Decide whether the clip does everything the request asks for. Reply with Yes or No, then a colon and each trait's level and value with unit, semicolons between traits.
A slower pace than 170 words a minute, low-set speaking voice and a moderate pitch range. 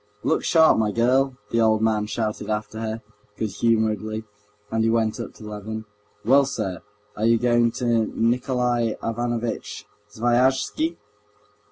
No: average, 140 wpm; low, 115 Hz; narrow, 1.9 semitones